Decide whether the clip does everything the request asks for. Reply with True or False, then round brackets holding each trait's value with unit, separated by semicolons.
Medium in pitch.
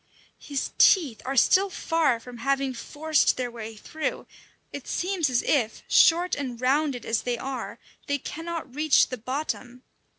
False (275 Hz)